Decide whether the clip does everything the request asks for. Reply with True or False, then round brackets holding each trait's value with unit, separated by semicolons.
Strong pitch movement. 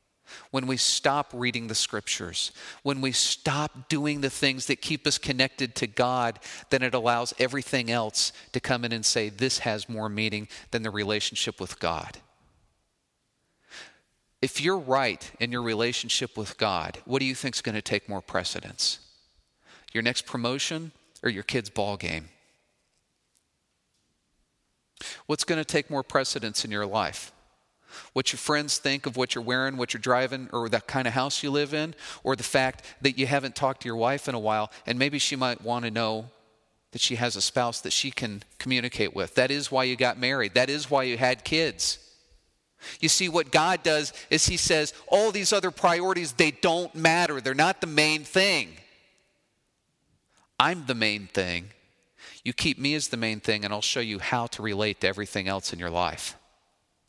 False (4.4 semitones)